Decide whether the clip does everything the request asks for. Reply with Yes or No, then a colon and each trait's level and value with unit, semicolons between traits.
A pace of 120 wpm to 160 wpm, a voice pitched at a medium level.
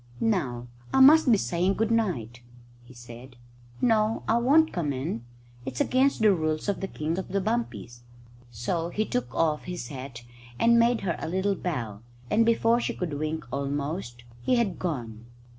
No: average, 175 wpm; medium, 170 Hz